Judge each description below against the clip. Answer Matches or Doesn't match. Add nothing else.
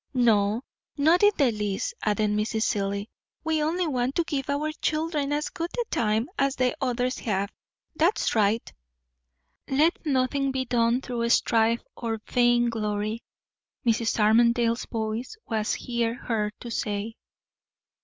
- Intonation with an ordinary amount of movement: Matches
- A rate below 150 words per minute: Matches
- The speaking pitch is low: Doesn't match